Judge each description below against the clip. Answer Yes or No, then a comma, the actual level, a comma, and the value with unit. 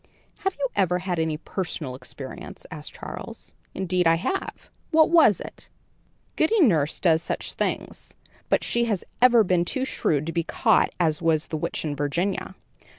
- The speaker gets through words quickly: No, average, 165 wpm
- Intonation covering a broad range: Yes, wide, 5.8 semitones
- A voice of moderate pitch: Yes, medium, 175 Hz